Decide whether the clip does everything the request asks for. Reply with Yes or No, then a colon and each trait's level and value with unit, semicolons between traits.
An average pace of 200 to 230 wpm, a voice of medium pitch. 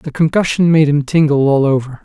Yes: fast, 205 wpm; medium, 150 Hz